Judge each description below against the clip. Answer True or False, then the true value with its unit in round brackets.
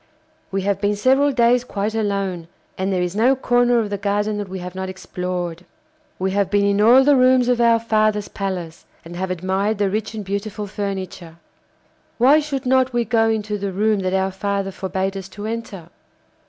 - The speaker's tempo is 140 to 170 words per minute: False (195 wpm)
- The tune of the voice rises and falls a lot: False (3.3 semitones)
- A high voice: True (205 Hz)